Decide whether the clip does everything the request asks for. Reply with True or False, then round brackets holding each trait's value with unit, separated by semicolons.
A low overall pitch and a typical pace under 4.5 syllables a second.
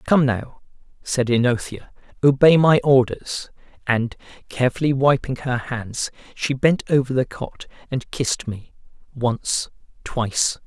True (130 Hz; 4.1 syllables/s)